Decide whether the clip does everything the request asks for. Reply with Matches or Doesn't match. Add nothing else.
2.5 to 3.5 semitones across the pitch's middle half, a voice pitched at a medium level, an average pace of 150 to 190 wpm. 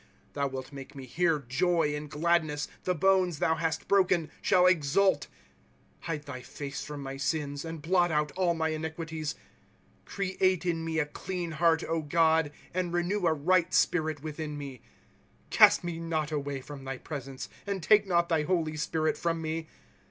Matches